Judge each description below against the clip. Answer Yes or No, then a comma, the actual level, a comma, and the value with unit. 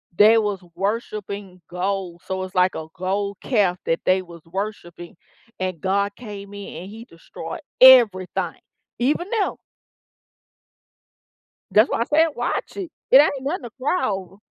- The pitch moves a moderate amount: Yes, average, 4.1 semitones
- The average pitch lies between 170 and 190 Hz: No, high, 200 Hz